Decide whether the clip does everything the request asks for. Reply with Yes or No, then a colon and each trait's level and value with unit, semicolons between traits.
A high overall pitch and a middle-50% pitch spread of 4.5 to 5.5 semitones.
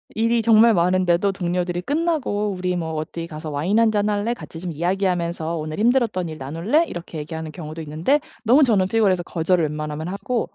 No: medium, 180 Hz; average, 5.1 semitones